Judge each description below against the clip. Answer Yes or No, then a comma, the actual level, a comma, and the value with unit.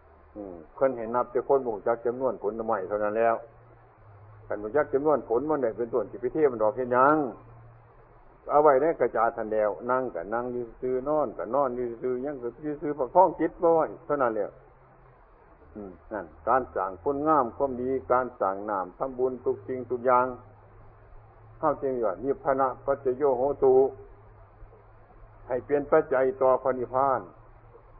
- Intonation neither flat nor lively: Yes, average, 3.6 semitones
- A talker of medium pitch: No, low, 125 Hz